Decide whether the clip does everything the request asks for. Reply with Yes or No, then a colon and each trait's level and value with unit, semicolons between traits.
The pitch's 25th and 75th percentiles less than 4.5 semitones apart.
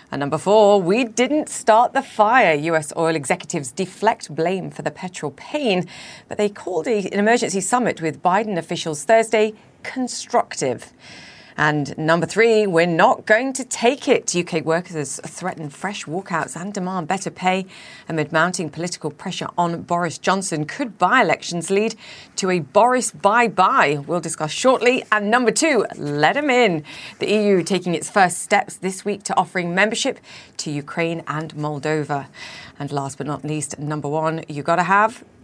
No: average, 5.2 semitones